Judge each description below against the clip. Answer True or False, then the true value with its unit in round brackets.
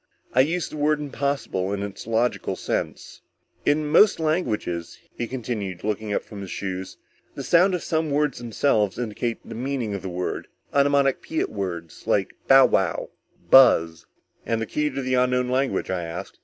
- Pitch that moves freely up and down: True (6.2 semitones)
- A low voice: True (120 Hz)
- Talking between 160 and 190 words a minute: True (165 wpm)